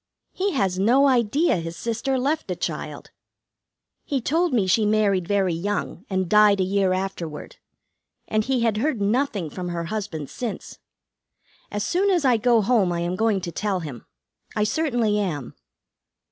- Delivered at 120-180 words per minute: Yes, average, 165 wpm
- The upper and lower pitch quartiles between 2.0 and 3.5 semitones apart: No, average, 5.1 semitones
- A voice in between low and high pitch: No, high, 210 Hz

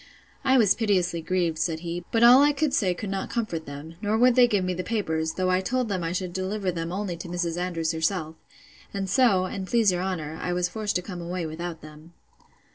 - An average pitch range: Yes, average, 3.6 semitones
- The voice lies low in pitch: No, medium, 185 Hz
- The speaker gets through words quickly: Yes, fast, 230 wpm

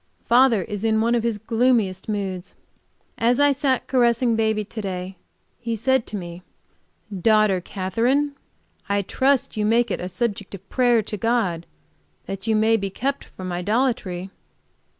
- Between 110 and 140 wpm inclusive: No, average, 155 wpm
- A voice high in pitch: Yes, high, 220 Hz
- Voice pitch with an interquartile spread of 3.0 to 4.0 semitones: Yes, average, 3.7 semitones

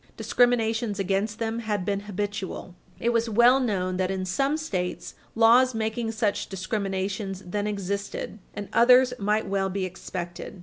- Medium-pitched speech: No, high, 205 Hz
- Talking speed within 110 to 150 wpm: Yes, average, 145 wpm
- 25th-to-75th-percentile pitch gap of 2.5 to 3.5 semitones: Yes, average, 2.9 semitones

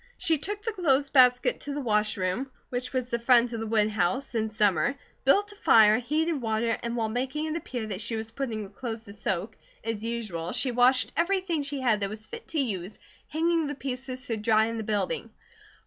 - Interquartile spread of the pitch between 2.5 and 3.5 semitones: No, average, 4.3 semitones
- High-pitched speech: Yes, high, 235 Hz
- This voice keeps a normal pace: No, fast, 210 wpm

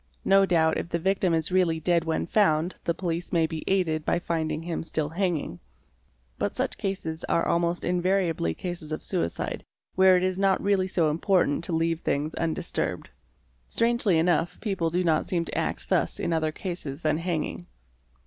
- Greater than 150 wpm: Yes, average, 175 wpm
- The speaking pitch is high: No, medium, 170 Hz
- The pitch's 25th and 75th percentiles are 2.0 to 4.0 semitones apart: Yes, narrow, 2.4 semitones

